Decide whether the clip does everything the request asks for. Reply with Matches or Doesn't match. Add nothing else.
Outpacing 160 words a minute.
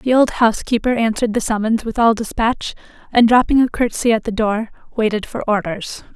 Matches